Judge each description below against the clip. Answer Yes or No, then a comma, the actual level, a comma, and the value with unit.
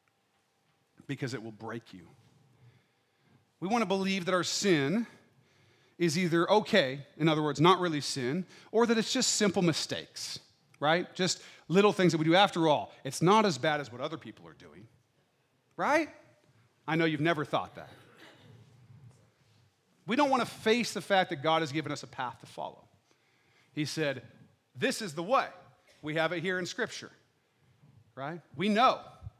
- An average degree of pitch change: No, wide, 6.3 semitones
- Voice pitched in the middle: Yes, medium, 155 Hz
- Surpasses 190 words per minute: No, average, 170 wpm